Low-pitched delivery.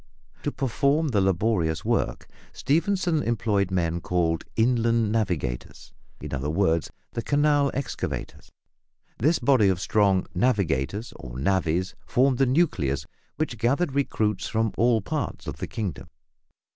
Yes: low, 110 Hz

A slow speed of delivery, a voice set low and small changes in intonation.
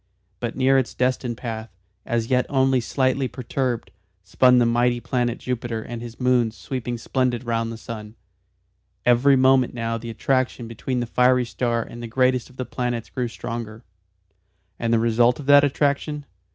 No: average, 165 wpm; low, 120 Hz; narrow, 1.9 semitones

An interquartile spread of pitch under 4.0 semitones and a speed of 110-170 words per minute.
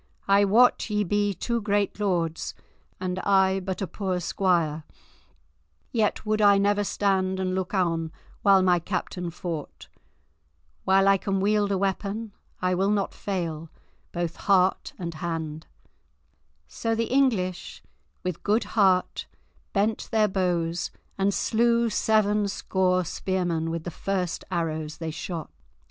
Yes: average, 2.8 semitones; slow, 135 wpm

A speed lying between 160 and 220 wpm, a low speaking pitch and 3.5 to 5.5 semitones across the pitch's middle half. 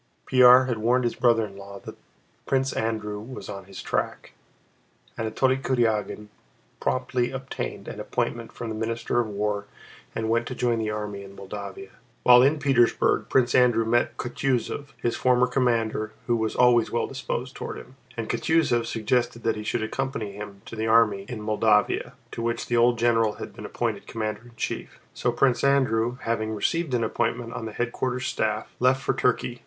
No: average, 180 wpm; low, 115 Hz; narrow, 2.5 semitones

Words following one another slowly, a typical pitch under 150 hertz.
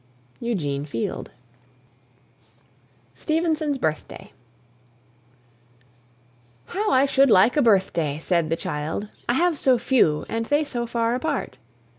No: slow, 110 wpm; high, 235 Hz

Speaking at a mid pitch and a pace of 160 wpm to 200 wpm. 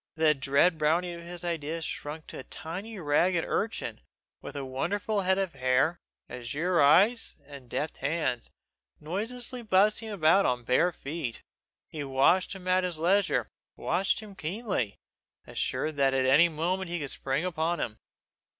No: medium, 165 Hz; average, 150 wpm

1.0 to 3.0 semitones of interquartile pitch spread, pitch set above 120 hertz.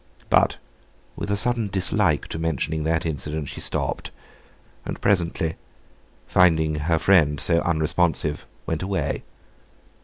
No: average, 2.7 semitones; very low, 80 Hz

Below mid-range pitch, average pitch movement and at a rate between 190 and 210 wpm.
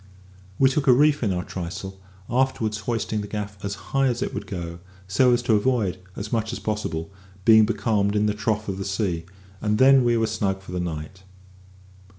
Yes: low, 105 Hz; average, 3.6 semitones; average, 200 wpm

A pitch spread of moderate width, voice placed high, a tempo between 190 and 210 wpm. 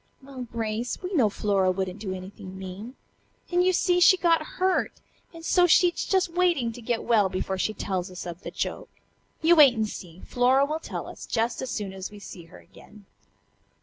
No: wide, 9.0 semitones; high, 230 Hz; average, 200 wpm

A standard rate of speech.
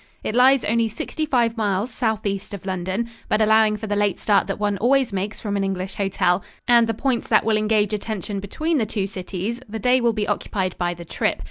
No: fast, 220 wpm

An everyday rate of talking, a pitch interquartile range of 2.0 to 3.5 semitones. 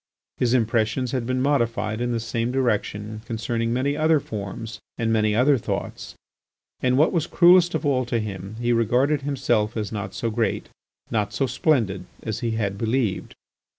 Yes: average, 170 wpm; average, 3.1 semitones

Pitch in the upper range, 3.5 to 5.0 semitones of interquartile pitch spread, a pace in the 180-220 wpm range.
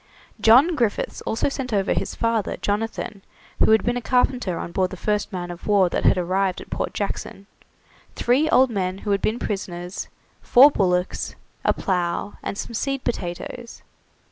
No: high, 205 Hz; average, 4.5 semitones; average, 170 wpm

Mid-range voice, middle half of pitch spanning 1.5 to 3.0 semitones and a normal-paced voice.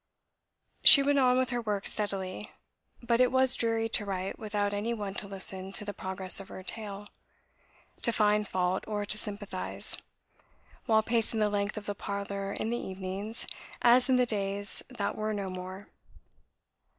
No: high, 205 Hz; narrow, 2.5 semitones; average, 170 wpm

